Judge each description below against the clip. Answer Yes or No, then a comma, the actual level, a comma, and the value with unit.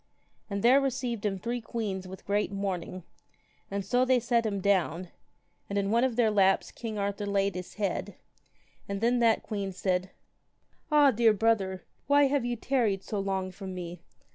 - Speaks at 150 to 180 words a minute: Yes, average, 175 wpm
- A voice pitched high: Yes, high, 205 Hz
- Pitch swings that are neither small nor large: Yes, average, 3.5 semitones